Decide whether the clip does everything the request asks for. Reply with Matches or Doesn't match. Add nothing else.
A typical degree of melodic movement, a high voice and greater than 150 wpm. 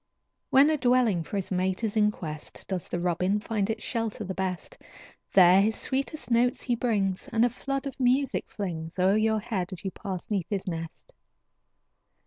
Matches